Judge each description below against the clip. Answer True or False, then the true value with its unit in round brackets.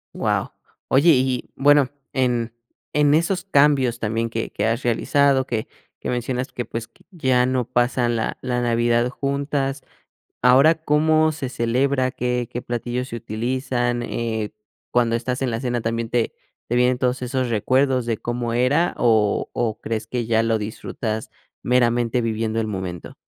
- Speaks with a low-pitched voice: True (120 Hz)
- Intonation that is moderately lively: False (2.2 semitones)